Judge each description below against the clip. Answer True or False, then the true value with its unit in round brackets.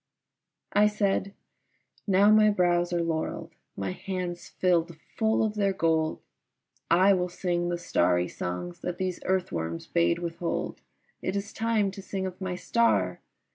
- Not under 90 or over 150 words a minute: True (145 wpm)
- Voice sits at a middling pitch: True (180 Hz)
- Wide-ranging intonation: False (2.9 semitones)